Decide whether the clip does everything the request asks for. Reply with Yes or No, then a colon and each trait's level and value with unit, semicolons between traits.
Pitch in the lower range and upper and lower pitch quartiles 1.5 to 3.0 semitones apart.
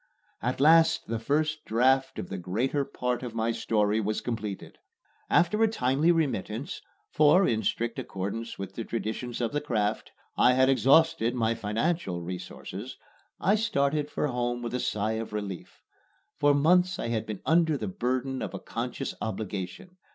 No: low, 120 Hz; average, 5.2 semitones